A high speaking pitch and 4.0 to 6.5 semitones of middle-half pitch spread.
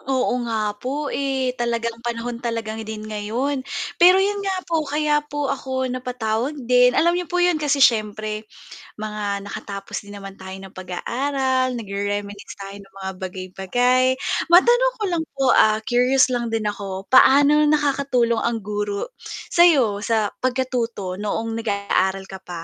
Yes: high, 235 Hz; average, 5.0 semitones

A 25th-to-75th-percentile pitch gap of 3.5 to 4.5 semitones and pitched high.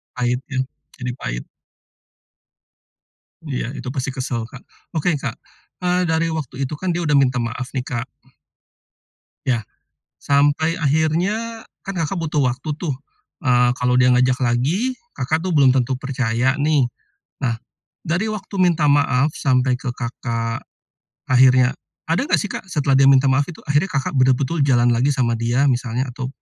No: average, 3.9 semitones; low, 135 Hz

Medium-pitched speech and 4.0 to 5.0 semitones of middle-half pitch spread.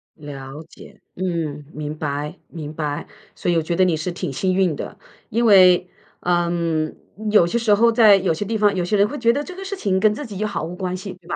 Yes: medium, 180 Hz; average, 4.6 semitones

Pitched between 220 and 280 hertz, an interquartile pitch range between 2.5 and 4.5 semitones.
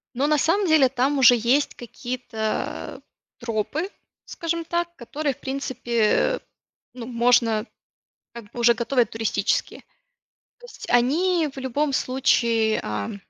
Yes: very high, 255 Hz; average, 4.2 semitones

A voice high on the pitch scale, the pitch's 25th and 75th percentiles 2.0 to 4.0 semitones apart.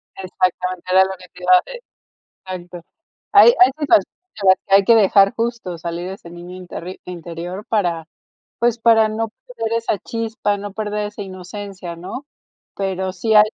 Yes: high, 195 Hz; average, 3.4 semitones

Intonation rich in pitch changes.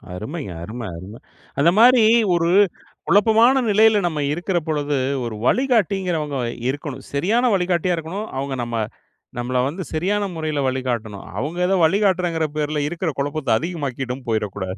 Yes: wide, 6.3 semitones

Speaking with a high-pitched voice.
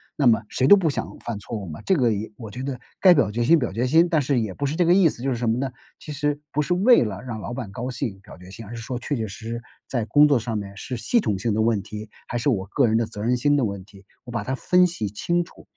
No: low, 120 Hz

